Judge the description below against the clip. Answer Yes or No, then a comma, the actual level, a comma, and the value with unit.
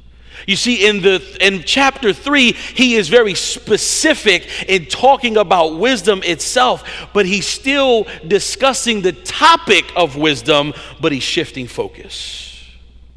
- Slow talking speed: Yes, slow, 130 wpm